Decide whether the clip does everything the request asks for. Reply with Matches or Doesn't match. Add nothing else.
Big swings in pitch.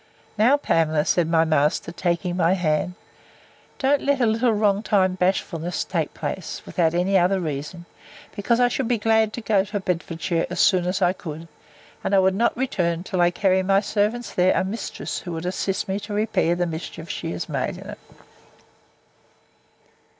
Doesn't match